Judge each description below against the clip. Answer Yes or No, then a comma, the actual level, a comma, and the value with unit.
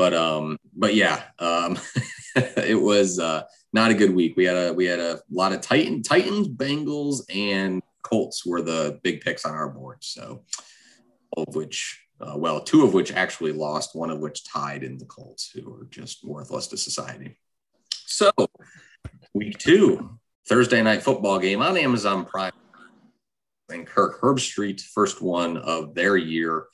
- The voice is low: Yes, very low, 90 Hz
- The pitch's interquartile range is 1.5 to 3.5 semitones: No, average, 5.2 semitones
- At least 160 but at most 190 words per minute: Yes, average, 170 wpm